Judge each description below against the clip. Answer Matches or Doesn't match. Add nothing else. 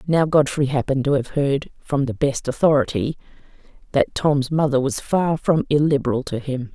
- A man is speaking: Doesn't match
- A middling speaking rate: Matches